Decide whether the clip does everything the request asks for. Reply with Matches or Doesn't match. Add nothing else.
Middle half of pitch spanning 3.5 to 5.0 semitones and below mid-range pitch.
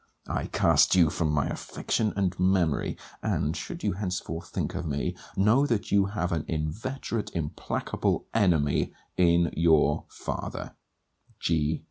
Matches